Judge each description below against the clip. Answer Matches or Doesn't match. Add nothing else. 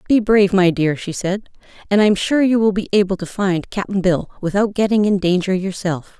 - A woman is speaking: Matches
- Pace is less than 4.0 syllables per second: Doesn't match